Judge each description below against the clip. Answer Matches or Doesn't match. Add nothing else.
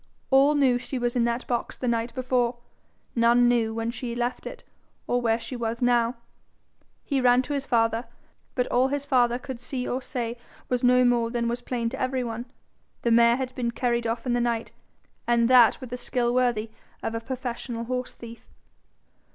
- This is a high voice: Matches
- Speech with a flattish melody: Matches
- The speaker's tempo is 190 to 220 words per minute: Matches